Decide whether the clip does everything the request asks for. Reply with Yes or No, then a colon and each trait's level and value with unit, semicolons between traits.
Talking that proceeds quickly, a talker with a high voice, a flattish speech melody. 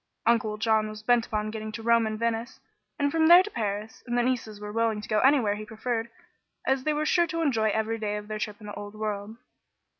Yes: fast, 240 wpm; high, 220 Hz; narrow, 2.3 semitones